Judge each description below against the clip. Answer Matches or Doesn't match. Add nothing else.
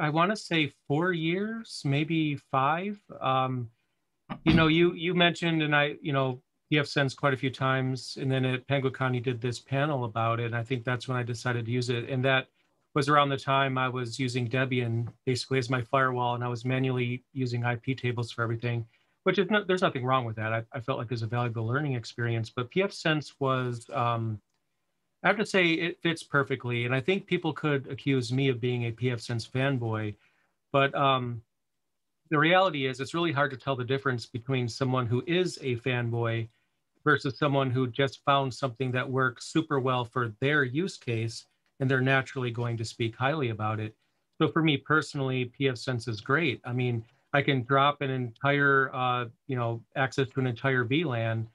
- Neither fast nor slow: Doesn't match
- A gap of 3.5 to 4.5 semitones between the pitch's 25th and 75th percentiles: Doesn't match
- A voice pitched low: Matches